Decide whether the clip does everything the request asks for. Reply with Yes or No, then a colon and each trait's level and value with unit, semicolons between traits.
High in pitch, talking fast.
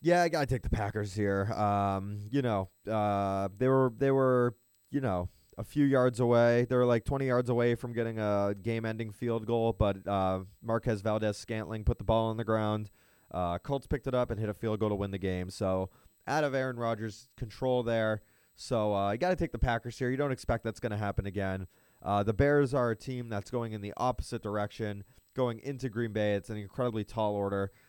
No: low, 115 Hz; fast, 215 wpm